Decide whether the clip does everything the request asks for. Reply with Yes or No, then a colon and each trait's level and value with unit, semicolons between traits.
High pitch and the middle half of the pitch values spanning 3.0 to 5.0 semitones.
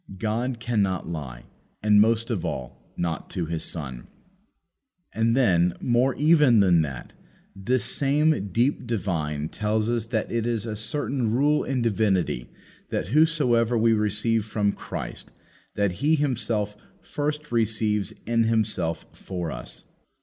No: low, 110 Hz; average, 4.2 semitones